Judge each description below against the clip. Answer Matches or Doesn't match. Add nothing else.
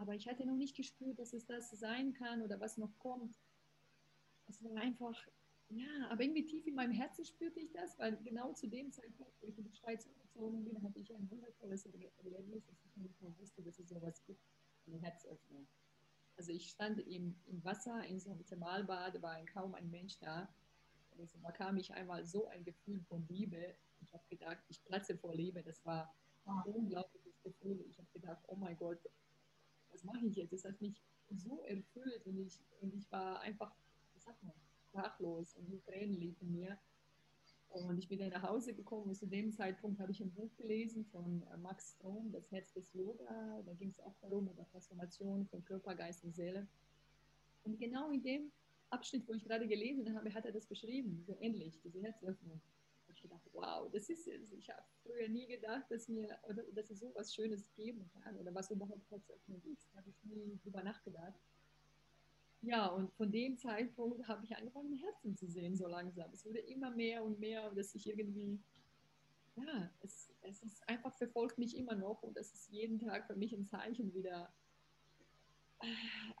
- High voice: Matches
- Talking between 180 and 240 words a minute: Matches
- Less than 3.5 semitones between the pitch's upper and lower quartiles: Doesn't match